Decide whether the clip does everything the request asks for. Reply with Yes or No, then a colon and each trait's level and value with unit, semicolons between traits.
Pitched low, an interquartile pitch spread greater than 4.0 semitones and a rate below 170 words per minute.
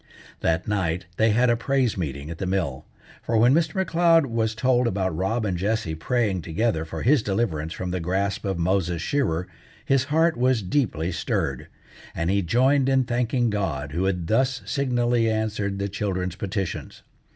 No: low, 105 Hz; wide, 5.4 semitones; average, 175 wpm